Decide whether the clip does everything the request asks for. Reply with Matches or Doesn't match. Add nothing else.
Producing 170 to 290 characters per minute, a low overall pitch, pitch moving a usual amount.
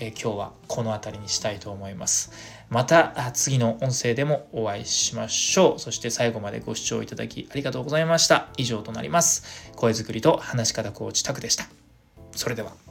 Doesn't match